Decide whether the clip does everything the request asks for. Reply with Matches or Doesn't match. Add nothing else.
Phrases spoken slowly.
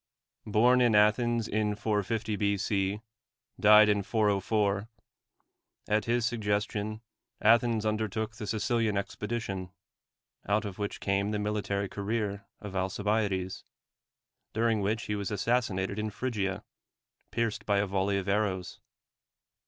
Matches